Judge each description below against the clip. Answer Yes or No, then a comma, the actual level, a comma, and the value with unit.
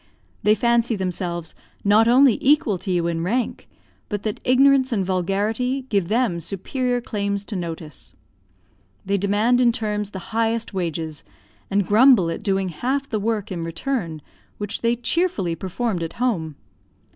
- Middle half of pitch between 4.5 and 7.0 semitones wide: Yes, average, 4.9 semitones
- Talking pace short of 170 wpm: Yes, average, 150 wpm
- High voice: Yes, high, 205 Hz